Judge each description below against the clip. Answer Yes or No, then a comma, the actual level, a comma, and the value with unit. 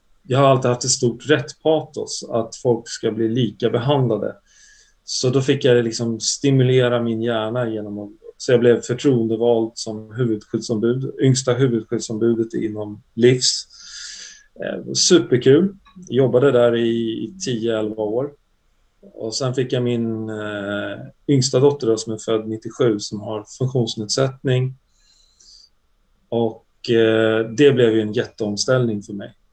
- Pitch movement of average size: Yes, average, 3.0 semitones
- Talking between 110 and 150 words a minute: Yes, slow, 125 wpm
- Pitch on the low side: Yes, low, 115 Hz